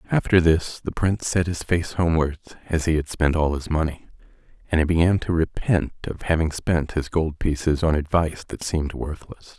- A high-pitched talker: No, very low, 80 Hz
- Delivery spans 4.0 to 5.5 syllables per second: Yes, 5.3 syllables/s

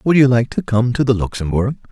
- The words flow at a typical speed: No, fast, 250 wpm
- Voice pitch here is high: No, low, 120 Hz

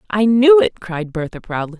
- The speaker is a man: No, female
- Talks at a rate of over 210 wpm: No, average, 200 wpm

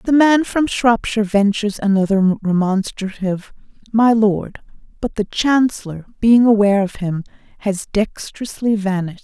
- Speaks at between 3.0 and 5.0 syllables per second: Yes, 4.9 syllables/s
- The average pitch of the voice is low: No, high, 210 Hz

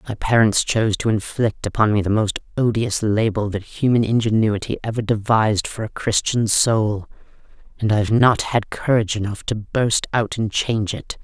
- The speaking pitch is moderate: No, low, 110 Hz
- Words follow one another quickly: No, average, 170 wpm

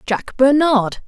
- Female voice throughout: Yes, female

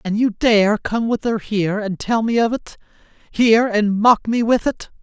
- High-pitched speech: Yes, high, 220 Hz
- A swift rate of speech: Yes, fast, 215 wpm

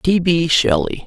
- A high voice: No, medium, 155 Hz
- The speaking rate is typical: Yes, average, 170 wpm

